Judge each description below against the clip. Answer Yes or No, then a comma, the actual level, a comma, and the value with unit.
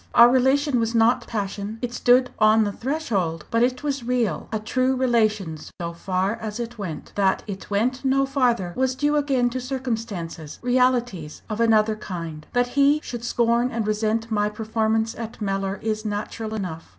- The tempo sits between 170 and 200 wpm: Yes, average, 175 wpm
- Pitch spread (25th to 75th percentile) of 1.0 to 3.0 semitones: No, average, 3.4 semitones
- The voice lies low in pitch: No, high, 225 Hz